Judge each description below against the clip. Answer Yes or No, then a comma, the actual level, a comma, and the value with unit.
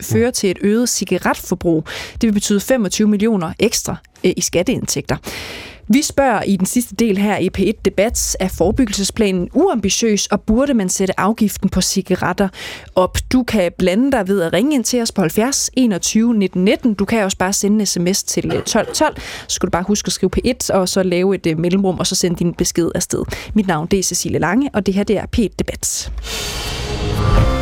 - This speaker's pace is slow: No, average, 195 wpm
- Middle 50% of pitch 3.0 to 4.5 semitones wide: Yes, average, 3.3 semitones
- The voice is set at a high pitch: Yes, high, 195 Hz